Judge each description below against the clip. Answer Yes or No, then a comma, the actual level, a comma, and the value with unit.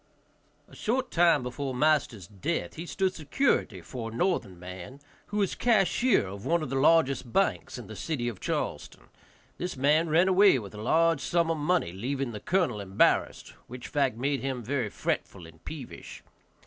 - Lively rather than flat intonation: Yes, wide, 6.8 semitones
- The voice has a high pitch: No, medium, 140 Hz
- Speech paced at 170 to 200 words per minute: Yes, average, 175 wpm